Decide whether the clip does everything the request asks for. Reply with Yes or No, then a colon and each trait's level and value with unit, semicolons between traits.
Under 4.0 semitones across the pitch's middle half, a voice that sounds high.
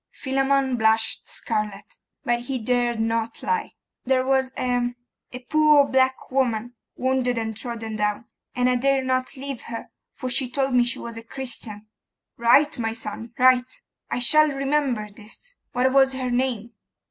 Yes: narrow, 2.6 semitones; very high, 250 Hz